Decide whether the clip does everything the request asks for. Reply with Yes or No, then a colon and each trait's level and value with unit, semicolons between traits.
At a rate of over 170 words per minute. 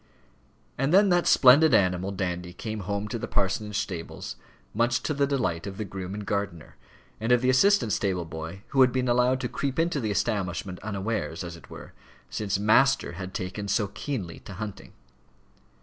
Yes: average, 180 wpm